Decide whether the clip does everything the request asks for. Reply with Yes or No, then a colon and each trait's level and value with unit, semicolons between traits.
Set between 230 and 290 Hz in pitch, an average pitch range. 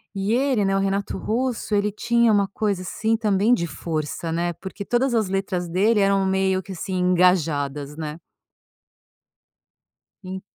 No: high, 195 Hz; average, 3.3 semitones